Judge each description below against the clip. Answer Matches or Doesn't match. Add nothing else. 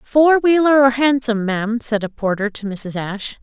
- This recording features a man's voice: Doesn't match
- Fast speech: Doesn't match